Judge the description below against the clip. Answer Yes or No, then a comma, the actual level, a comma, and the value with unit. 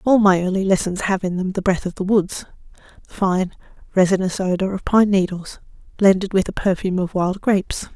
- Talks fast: No, average, 190 wpm